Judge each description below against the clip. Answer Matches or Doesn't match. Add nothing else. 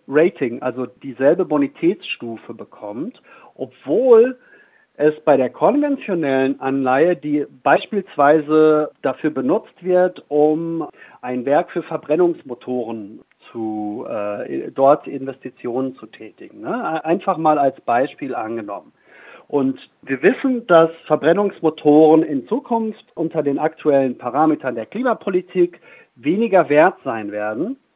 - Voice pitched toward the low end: Doesn't match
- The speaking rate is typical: Doesn't match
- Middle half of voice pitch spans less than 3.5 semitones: Doesn't match